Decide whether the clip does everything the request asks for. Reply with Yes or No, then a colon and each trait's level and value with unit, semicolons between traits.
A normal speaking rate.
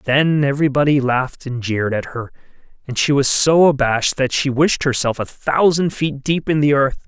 Yes: average, 195 wpm